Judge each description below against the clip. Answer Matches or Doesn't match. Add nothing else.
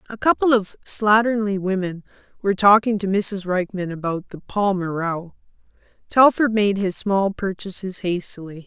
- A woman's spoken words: Matches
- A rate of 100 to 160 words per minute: Matches